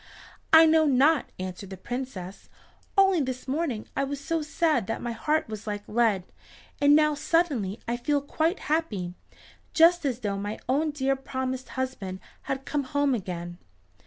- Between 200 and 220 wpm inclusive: No, average, 160 wpm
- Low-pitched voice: No, very high, 265 Hz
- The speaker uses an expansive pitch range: Yes, wide, 6.0 semitones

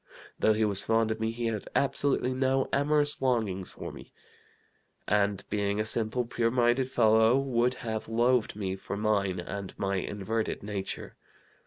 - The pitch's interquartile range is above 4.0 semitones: No, average, 3.3 semitones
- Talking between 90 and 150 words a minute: No, average, 160 wpm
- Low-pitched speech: Yes, low, 110 Hz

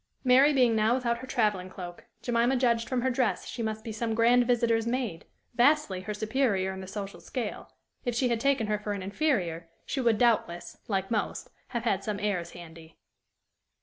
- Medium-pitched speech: No, high, 225 Hz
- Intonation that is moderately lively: Yes, average, 3.8 semitones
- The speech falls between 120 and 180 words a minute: No, average, 190 wpm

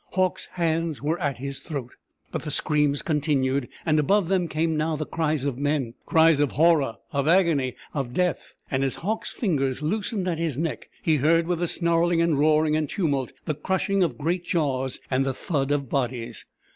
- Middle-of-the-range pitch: Yes, medium, 155 Hz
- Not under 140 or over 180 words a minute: No, average, 190 wpm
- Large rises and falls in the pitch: No, average, 3.3 semitones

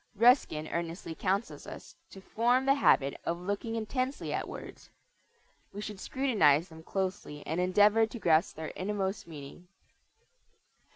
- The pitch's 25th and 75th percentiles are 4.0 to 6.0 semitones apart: Yes, wide, 5.4 semitones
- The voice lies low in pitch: No, high, 190 Hz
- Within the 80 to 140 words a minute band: Yes, slow, 135 wpm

